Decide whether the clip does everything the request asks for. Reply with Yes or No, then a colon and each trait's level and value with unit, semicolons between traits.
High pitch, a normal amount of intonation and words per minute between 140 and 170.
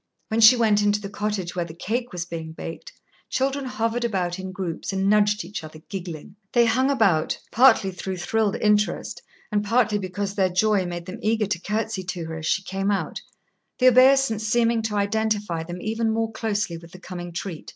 No: high, 205 Hz; average, 3.6 semitones; average, 195 wpm